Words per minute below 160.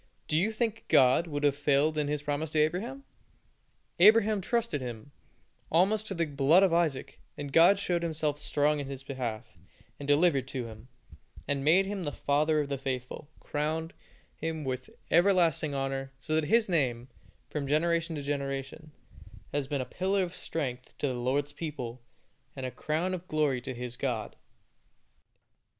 No: average, 165 wpm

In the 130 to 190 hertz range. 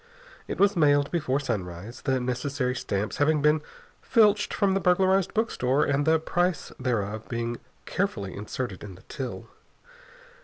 Yes: medium, 140 Hz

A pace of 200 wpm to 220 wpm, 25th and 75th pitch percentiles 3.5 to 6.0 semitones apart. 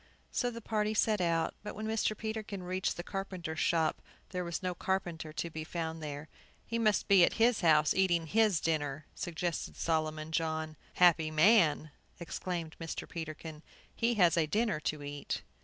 No: average, 170 wpm; average, 4.2 semitones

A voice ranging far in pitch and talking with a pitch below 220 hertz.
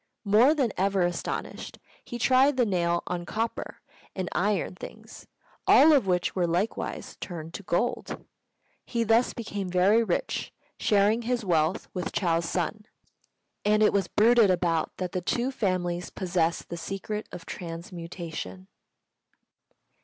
No: average, 4.3 semitones; high, 190 Hz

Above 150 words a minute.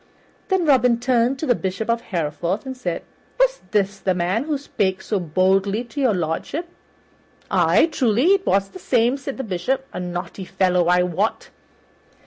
Yes: average, 170 wpm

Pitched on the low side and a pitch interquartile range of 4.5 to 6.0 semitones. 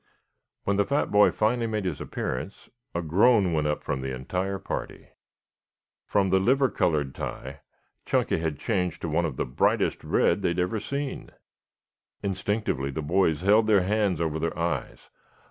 Yes: very low, 90 Hz; average, 4.8 semitones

